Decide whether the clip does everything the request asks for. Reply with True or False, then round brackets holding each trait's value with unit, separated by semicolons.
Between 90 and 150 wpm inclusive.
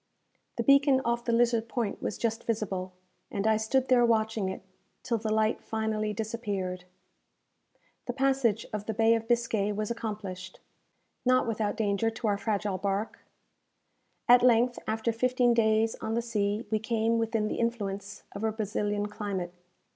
False (160 wpm)